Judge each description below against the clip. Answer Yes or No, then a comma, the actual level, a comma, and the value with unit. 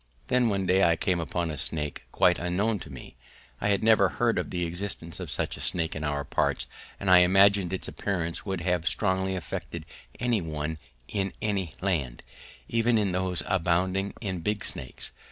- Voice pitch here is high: No, very low, 90 Hz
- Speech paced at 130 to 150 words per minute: No, average, 185 wpm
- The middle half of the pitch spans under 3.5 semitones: Yes, average, 3.0 semitones